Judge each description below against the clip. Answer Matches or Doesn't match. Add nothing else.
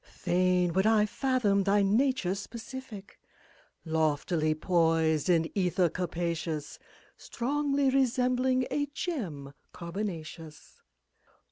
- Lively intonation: Matches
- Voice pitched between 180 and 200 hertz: Matches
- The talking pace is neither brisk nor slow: Doesn't match